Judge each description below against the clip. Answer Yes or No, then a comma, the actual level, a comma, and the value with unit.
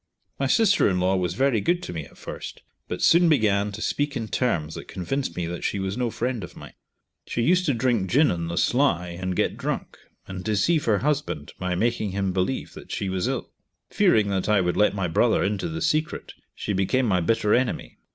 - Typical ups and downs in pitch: No, wide, 6.1 semitones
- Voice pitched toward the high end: No, low, 105 Hz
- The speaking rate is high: Yes, fast, 220 wpm